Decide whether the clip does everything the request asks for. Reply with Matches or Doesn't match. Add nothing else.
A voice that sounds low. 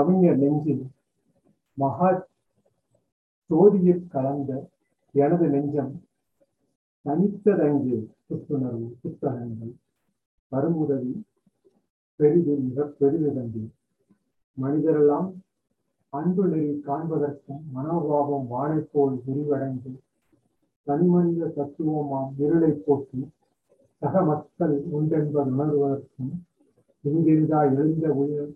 Doesn't match